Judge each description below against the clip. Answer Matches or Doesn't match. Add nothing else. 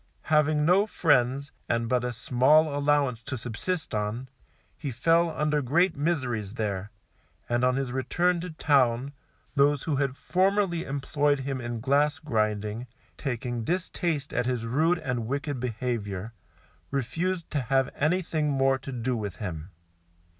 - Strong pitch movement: Doesn't match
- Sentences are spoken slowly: Doesn't match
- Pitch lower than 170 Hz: Matches